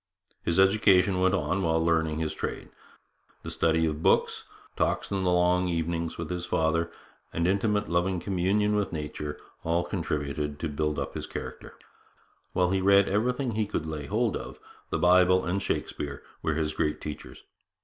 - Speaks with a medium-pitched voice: No, very low, 85 Hz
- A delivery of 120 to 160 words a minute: No, average, 170 wpm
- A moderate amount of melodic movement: Yes, average, 3.2 semitones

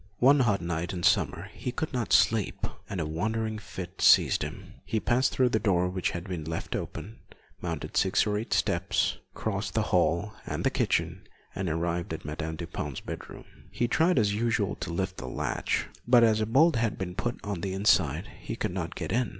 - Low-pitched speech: Yes, low, 100 Hz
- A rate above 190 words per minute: Yes, average, 200 wpm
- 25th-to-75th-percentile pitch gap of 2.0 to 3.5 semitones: No, average, 4.8 semitones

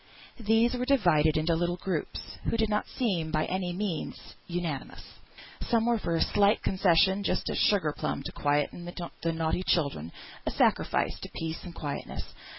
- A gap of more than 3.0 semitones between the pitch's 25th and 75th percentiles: Yes, average, 4.5 semitones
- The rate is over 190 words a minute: No, average, 165 wpm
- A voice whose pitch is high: No, medium, 175 Hz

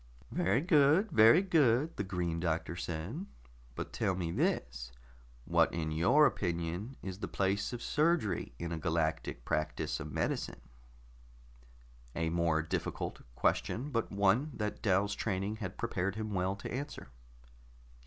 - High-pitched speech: No, very low, 95 Hz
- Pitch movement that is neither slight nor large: No, wide, 6.5 semitones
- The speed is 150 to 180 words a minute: No, average, 140 wpm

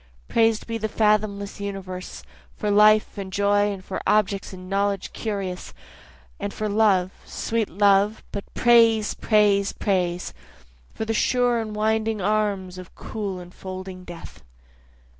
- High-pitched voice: Yes, high, 205 Hz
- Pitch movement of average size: No, narrow, 2.2 semitones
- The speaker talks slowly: Yes, slow, 130 wpm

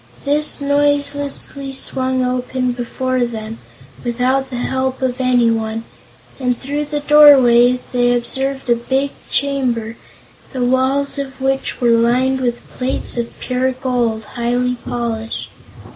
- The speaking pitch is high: Yes, very high, 255 Hz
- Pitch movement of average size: No, narrow, 2.0 semitones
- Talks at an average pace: No, slow, 125 wpm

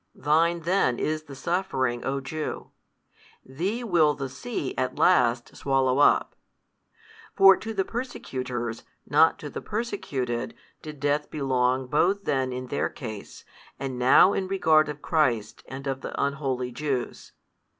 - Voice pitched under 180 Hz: Yes, medium, 140 Hz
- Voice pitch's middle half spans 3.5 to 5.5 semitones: Yes, average, 4.5 semitones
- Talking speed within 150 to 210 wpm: No, average, 140 wpm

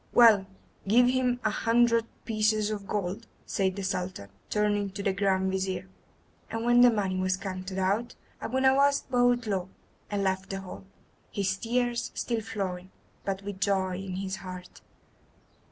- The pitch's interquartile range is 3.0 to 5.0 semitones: Yes, average, 3.4 semitones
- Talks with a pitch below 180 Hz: No, high, 200 Hz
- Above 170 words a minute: No, average, 155 wpm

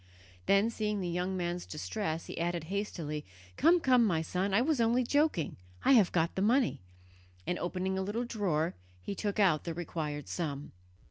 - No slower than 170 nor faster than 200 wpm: Yes, average, 180 wpm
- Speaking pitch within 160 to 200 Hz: Yes, high, 190 Hz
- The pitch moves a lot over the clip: No, average, 4.8 semitones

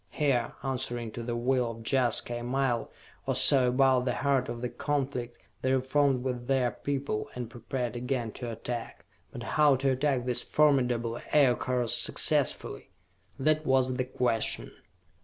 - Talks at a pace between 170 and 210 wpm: No, average, 155 wpm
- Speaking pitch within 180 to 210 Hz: No, low, 125 Hz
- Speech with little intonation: Yes, narrow, 1.9 semitones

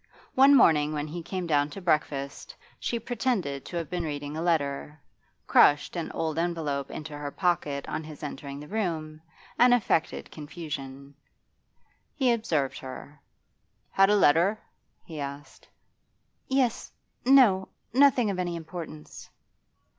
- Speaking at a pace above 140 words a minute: No, slow, 135 wpm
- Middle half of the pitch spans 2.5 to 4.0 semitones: No, average, 4.8 semitones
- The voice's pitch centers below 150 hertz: No, medium, 160 Hz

